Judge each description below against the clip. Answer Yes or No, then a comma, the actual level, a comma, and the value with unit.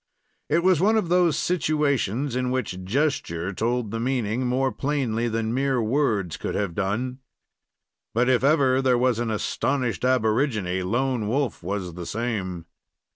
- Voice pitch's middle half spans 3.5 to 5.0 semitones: Yes, average, 4.2 semitones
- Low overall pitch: Yes, low, 125 Hz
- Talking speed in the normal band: Yes, average, 150 wpm